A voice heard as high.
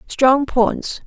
Yes: very high, 260 Hz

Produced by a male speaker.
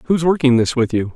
Yes: male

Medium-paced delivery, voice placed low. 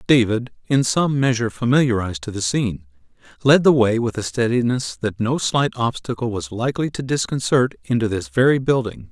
Yes: average, 170 wpm; low, 120 Hz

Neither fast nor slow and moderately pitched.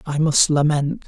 Yes: average, 170 wpm; medium, 150 Hz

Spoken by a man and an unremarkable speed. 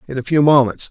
No: male; fast, 265 wpm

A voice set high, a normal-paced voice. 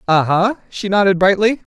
Yes: high, 195 Hz; average, 170 wpm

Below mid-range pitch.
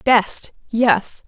No: high, 225 Hz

